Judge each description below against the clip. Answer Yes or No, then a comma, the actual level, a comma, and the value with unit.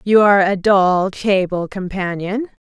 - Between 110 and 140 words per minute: Yes, slow, 135 wpm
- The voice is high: Yes, high, 195 Hz